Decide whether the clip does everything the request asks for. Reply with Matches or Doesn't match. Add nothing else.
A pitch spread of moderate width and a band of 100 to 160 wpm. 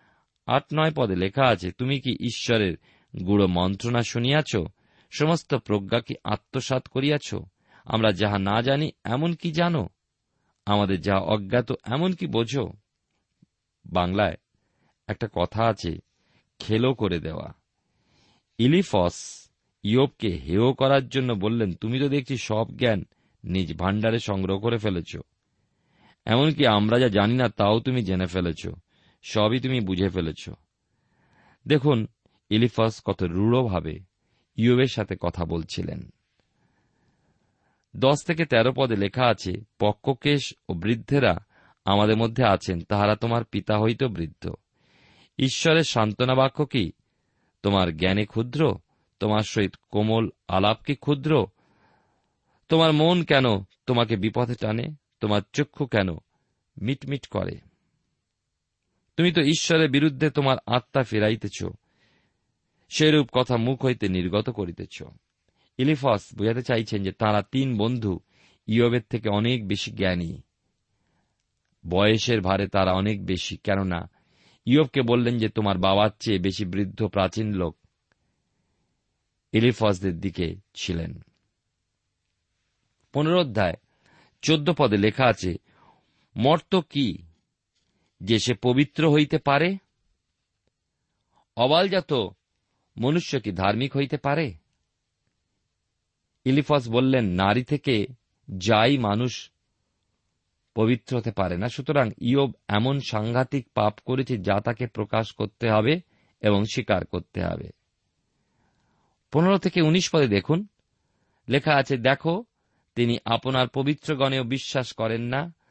Matches